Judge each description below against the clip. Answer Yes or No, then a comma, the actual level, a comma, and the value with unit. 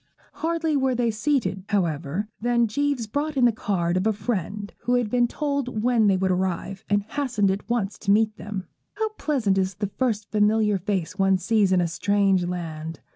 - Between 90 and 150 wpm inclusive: No, average, 190 wpm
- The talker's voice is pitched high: Yes, high, 210 Hz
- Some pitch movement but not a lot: Yes, average, 4.2 semitones